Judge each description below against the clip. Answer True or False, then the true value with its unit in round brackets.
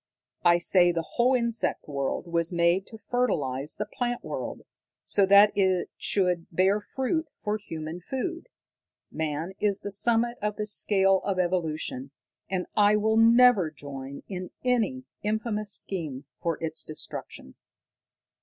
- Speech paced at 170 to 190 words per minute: False (140 wpm)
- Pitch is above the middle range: True (195 Hz)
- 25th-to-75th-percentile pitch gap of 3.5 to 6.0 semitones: True (4.7 semitones)